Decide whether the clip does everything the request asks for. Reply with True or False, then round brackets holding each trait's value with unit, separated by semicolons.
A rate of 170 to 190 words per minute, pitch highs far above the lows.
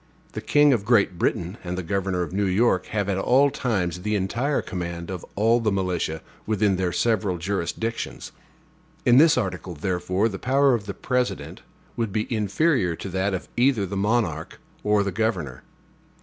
False (175 wpm; 4.1 semitones)